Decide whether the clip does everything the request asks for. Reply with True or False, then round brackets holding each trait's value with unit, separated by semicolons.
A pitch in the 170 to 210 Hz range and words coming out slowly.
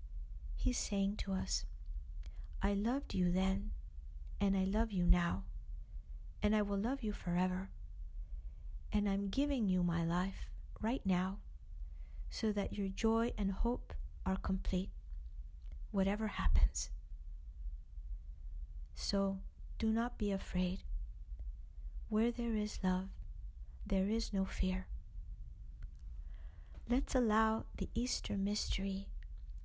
True (185 Hz; 110 wpm)